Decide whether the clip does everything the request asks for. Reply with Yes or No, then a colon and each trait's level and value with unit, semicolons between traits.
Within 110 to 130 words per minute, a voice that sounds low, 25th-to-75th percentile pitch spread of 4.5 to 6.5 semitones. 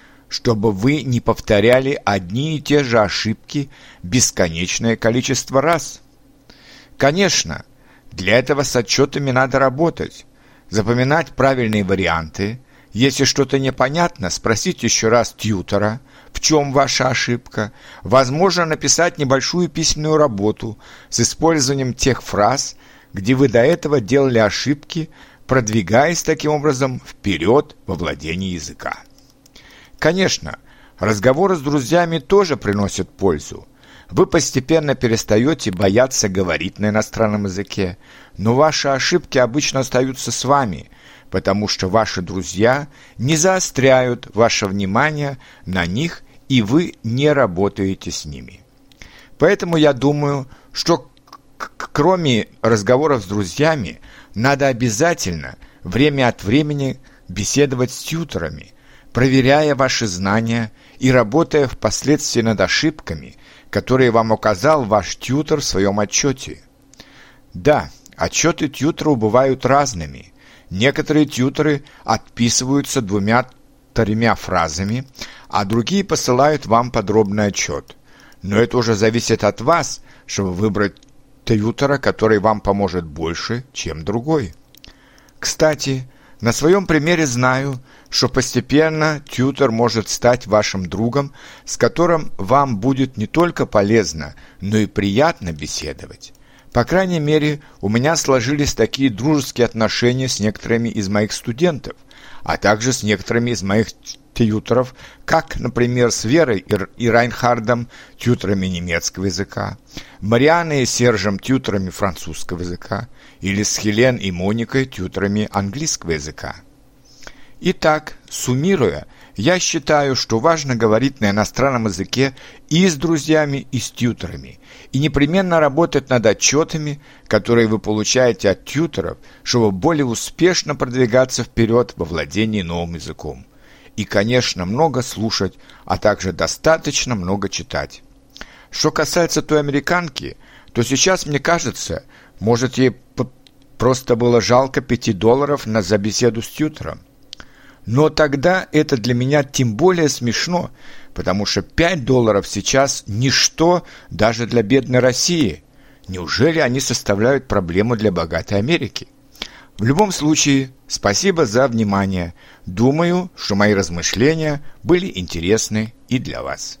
Yes: average, 120 wpm; low, 125 Hz; average, 5.2 semitones